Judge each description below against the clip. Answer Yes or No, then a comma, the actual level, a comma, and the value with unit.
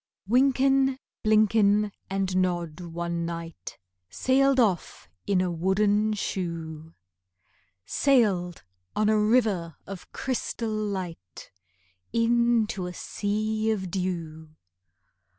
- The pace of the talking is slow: Yes, slow, 95 wpm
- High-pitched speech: Yes, high, 200 Hz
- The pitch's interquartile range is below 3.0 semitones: No, average, 4.2 semitones